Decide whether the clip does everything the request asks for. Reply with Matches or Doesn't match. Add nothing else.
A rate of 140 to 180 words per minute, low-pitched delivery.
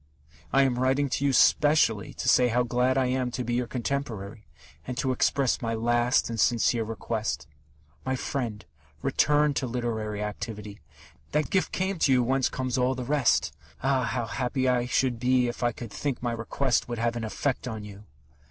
Doesn't match